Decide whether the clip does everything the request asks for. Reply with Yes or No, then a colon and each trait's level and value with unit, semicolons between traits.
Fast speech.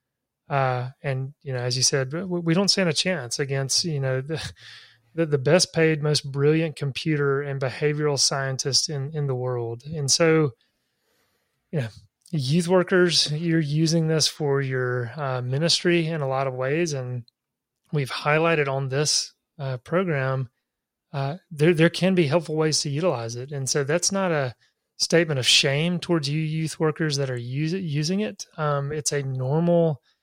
No: average, 170 wpm